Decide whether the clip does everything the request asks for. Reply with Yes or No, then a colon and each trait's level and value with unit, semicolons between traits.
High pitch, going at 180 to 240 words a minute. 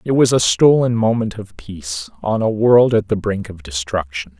No: low, 105 Hz; fast, 205 wpm